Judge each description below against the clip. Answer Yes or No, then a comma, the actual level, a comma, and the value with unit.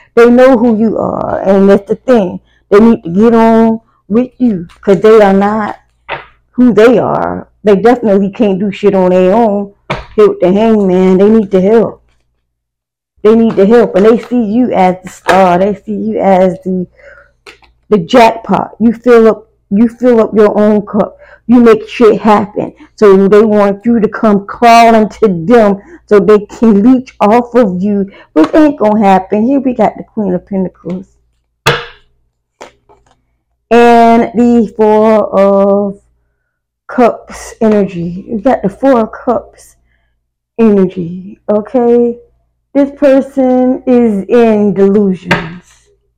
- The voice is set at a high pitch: Yes, high, 210 Hz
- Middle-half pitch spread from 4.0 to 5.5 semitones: No, average, 3.3 semitones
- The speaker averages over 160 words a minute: No, average, 150 wpm